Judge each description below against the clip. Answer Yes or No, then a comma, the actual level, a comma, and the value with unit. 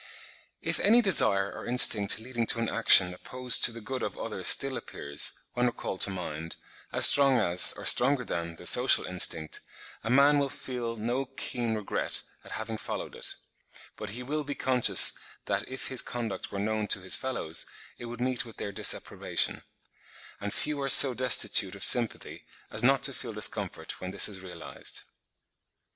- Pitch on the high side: No, low, 120 Hz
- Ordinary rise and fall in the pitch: Yes, average, 4.6 semitones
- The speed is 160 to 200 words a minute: Yes, average, 180 wpm